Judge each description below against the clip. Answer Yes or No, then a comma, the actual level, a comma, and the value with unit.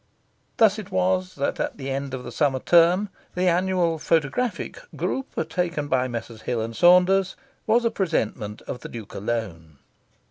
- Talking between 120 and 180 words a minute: Yes, average, 165 wpm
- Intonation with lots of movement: Yes, wide, 7.1 semitones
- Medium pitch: Yes, medium, 160 Hz